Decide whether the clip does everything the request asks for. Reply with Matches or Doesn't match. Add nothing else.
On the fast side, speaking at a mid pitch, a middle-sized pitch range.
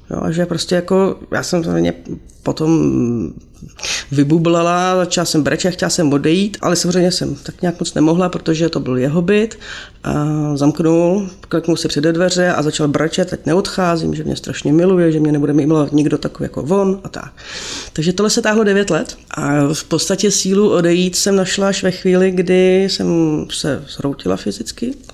Matches